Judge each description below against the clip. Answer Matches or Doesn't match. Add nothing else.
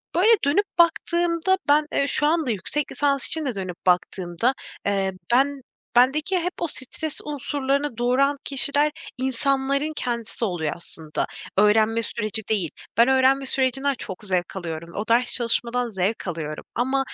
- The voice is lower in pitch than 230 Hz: Doesn't match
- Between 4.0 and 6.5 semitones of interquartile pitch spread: Matches